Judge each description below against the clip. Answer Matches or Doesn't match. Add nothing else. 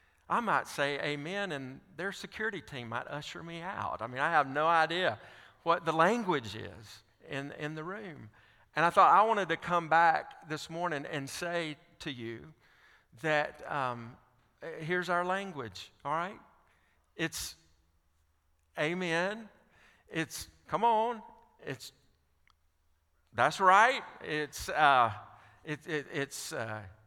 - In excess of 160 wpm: Doesn't match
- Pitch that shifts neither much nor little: Doesn't match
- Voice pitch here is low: Doesn't match